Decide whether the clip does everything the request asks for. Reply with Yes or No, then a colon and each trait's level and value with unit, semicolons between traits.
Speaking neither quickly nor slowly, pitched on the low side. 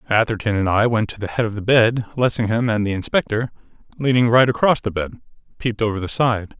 No: fast, 210 wpm; low, 110 Hz